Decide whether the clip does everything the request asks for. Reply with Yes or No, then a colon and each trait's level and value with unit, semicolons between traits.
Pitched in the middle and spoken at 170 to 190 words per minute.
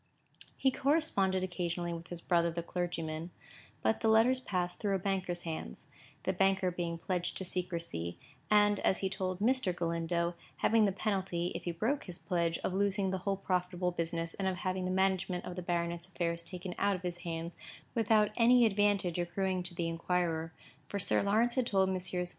Yes: medium, 180 Hz; average, 185 wpm